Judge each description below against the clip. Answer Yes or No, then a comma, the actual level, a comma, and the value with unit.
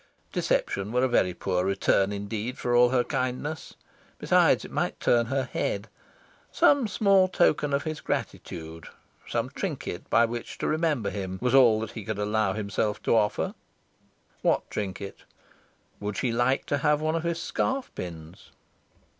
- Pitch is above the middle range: No, low, 120 Hz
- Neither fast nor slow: Yes, average, 160 wpm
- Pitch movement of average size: No, wide, 6.1 semitones